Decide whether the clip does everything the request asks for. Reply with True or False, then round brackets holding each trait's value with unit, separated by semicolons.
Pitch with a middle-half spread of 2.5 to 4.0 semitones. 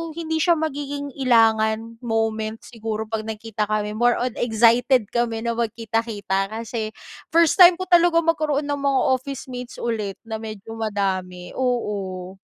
True (3.3 semitones)